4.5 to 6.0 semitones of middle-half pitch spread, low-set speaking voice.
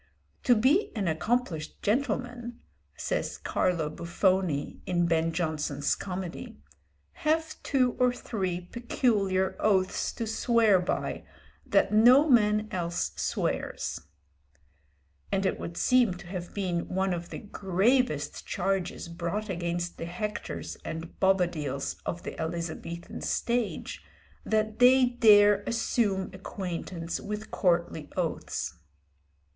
No: average, 4.8 semitones; high, 190 Hz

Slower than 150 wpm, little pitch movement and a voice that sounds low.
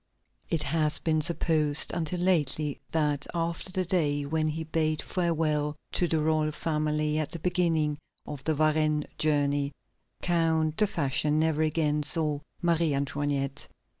No: average, 140 wpm; narrow, 1.7 semitones; medium, 155 Hz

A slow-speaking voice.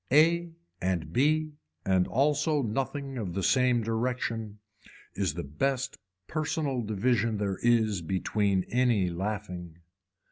Yes: slow, 115 wpm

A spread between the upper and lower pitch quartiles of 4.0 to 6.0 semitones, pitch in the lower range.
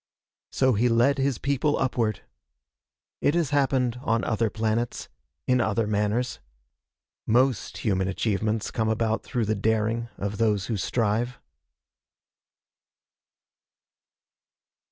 No: average, 2.7 semitones; low, 115 Hz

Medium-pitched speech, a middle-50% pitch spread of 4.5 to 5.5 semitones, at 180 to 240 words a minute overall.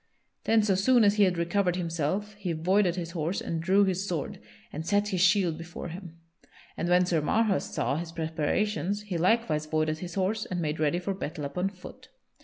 No: medium, 180 Hz; average, 3.6 semitones; average, 200 wpm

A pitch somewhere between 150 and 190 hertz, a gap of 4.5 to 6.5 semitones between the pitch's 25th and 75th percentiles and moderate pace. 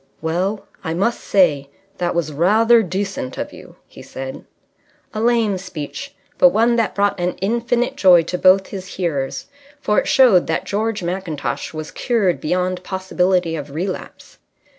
No: medium, 185 Hz; average, 3.9 semitones; average, 155 wpm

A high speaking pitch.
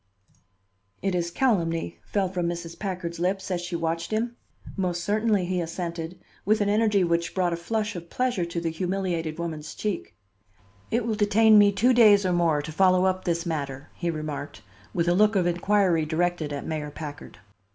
No: medium, 175 Hz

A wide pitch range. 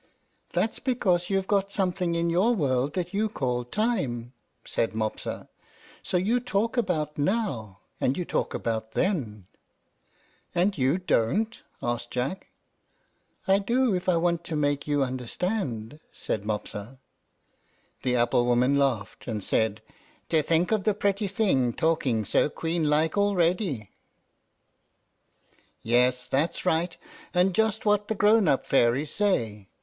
Yes: wide, 8.0 semitones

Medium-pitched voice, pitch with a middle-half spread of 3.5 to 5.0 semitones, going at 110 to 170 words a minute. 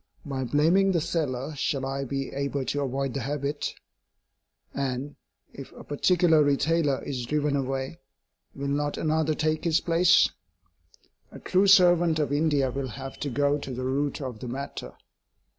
No: medium, 145 Hz; narrow, 2.6 semitones; average, 160 wpm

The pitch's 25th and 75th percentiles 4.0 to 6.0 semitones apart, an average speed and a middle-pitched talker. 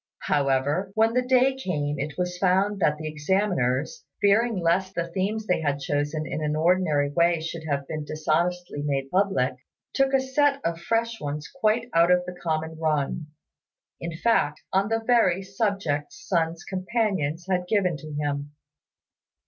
Yes: average, 5.0 semitones; average, 160 wpm; medium, 175 Hz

